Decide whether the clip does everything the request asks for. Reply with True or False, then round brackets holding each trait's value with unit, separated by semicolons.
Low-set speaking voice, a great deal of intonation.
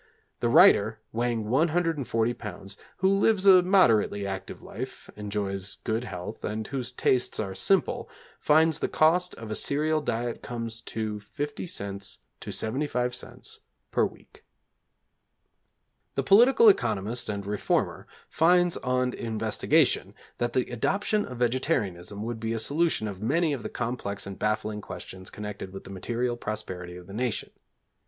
True (115 Hz; 6.0 semitones)